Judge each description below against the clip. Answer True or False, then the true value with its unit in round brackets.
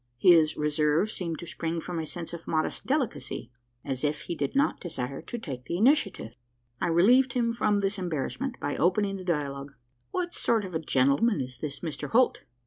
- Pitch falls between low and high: True (170 Hz)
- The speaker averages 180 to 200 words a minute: True (190 wpm)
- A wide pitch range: True (6.1 semitones)